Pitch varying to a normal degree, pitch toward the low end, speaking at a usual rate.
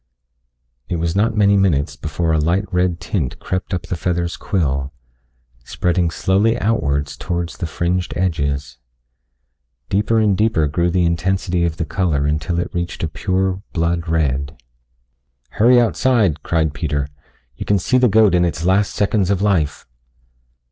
Yes: average, 3.6 semitones; very low, 85 Hz; average, 155 wpm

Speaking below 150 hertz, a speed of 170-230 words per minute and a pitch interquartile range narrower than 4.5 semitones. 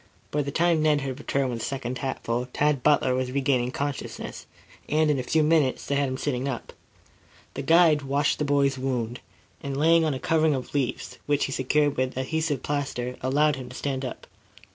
Yes: medium, 140 Hz; average, 200 wpm; narrow, 2.4 semitones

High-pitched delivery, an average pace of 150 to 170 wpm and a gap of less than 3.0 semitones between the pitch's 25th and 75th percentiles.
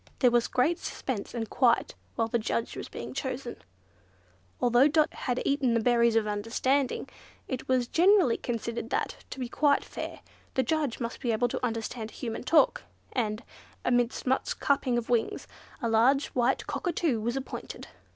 Yes: high, 245 Hz; average, 165 wpm; narrow, 2.5 semitones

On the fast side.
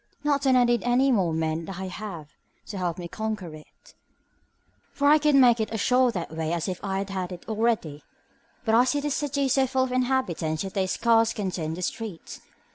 Yes: fast, 230 wpm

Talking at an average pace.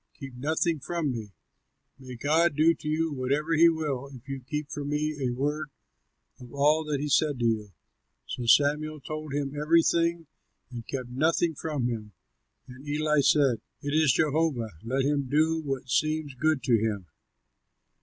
Yes: average, 165 wpm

